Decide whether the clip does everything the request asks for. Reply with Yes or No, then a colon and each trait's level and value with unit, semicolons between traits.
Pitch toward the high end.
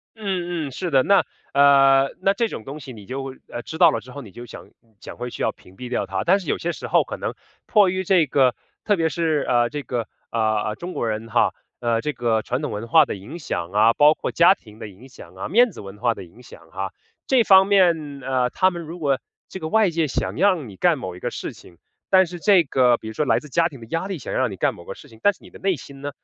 No: medium, 140 Hz